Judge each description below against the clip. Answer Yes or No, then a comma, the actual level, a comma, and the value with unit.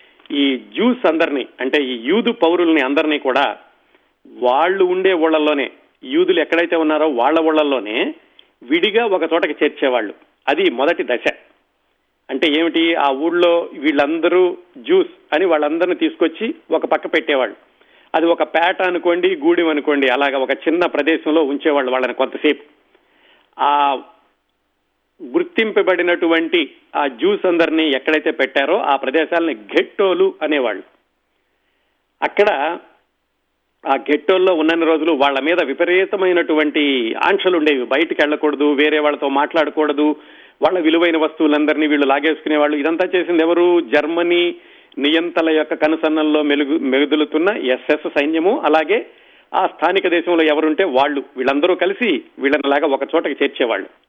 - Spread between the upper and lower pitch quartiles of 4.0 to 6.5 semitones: No, average, 3.3 semitones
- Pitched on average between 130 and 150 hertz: No, medium, 160 Hz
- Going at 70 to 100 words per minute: No, average, 115 wpm